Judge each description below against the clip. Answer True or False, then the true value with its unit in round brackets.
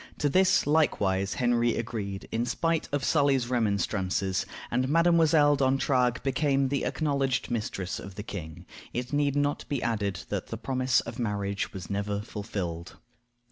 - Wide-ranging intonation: True (5.8 semitones)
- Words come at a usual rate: True (145 wpm)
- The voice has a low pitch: True (120 Hz)